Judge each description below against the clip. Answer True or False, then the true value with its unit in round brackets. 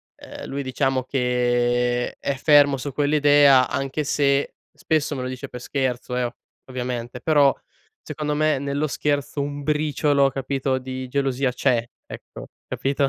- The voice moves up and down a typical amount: False (2.2 semitones)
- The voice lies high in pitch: False (135 Hz)